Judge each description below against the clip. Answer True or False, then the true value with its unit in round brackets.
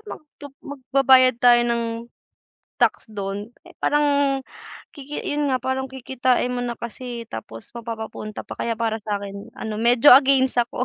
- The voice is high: True (245 Hz)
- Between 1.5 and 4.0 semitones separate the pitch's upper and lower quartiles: True (2.9 semitones)